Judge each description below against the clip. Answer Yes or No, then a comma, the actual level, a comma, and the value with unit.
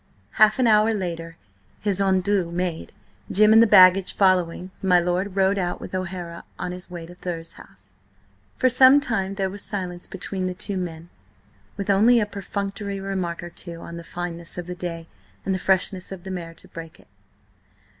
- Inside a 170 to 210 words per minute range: Yes, average, 185 wpm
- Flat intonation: Yes, narrow, 2.3 semitones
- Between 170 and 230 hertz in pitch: Yes, medium, 185 Hz